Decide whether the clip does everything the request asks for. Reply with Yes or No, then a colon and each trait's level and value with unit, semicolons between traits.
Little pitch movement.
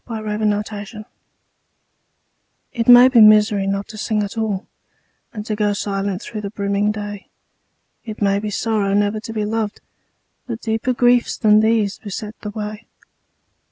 Yes: narrow, 1.4 semitones